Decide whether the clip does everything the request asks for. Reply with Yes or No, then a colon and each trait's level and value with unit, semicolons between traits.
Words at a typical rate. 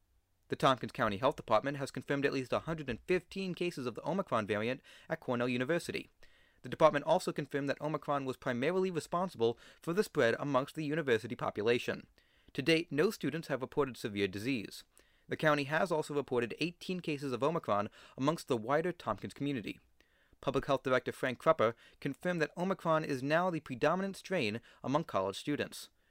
Yes: average, 165 wpm